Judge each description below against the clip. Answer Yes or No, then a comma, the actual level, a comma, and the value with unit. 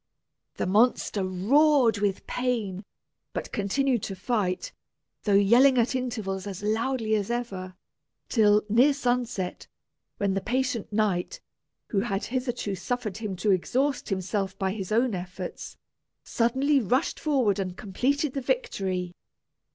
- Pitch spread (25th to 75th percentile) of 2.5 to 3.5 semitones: No, average, 4.6 semitones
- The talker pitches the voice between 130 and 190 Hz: No, high, 215 Hz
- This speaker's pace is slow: Yes, slow, 130 wpm